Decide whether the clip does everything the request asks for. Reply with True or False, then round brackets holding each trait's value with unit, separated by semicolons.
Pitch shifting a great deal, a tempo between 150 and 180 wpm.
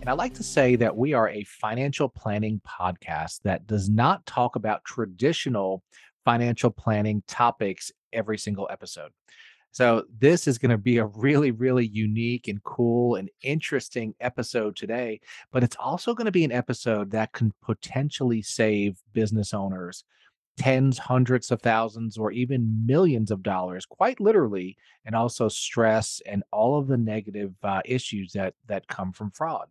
False (3.2 semitones; 160 wpm)